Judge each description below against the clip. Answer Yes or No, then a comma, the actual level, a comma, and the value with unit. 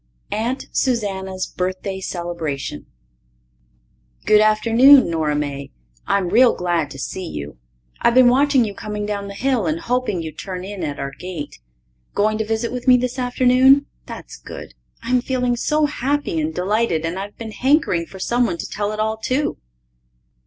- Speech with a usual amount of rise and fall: No, wide, 5.8 semitones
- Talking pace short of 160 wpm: No, average, 165 wpm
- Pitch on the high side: Yes, high, 215 Hz